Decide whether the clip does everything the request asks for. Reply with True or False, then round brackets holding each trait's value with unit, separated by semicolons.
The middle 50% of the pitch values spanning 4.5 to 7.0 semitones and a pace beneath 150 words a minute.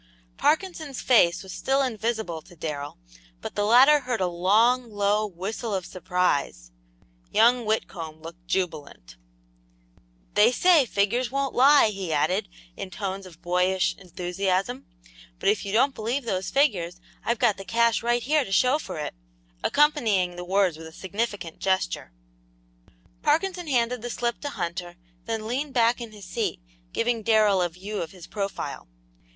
False (5.1 semitones; 155 wpm)